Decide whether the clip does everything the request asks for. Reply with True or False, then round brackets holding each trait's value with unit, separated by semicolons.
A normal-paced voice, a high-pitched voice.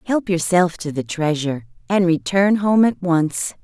False (165 wpm; 175 Hz)